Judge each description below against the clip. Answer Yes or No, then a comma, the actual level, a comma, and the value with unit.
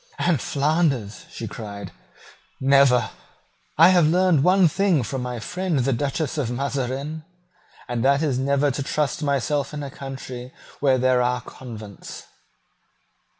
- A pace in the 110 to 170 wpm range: Yes, average, 140 wpm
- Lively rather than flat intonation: No, average, 3.4 semitones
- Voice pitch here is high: No, low, 135 Hz